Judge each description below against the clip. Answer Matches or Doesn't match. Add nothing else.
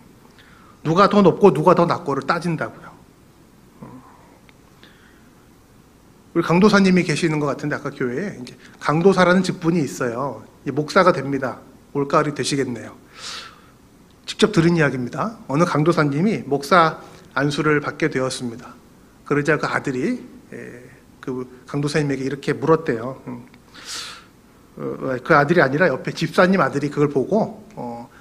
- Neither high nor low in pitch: Matches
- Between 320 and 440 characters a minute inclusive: Doesn't match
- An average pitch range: Matches